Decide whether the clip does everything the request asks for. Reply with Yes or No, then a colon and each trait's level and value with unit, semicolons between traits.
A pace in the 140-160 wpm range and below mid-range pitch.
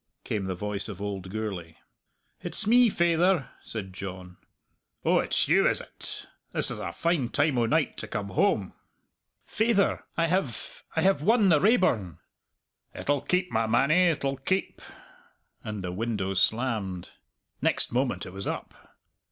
Yes: average, 150 wpm; low, 115 Hz